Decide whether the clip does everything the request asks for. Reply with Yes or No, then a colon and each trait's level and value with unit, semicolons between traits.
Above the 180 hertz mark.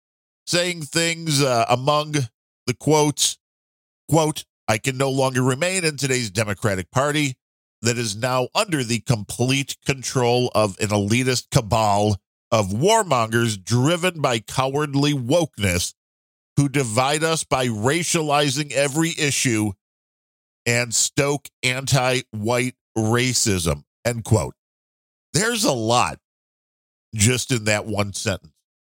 No: low, 125 Hz